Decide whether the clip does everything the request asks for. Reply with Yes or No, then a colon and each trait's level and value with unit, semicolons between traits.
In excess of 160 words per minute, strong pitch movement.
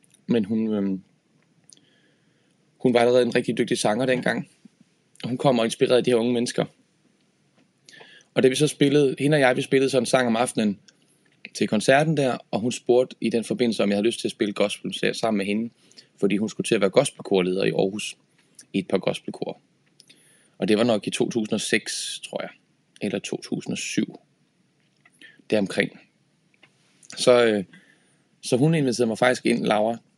No: average, 180 wpm; average, 3.7 semitones